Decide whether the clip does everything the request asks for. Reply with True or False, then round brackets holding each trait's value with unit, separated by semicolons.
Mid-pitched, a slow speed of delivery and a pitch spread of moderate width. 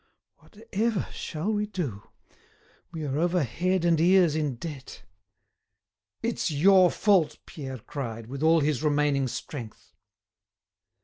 True (155 Hz; 120 wpm; 4.9 semitones)